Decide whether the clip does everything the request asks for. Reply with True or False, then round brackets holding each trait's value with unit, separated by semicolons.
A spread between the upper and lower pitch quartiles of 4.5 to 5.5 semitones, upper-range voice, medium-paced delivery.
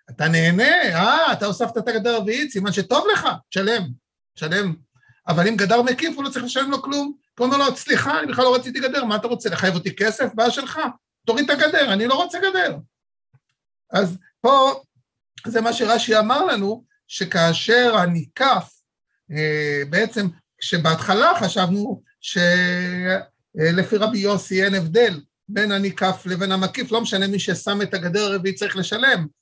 False (5.2 semitones; 205 Hz; 155 wpm)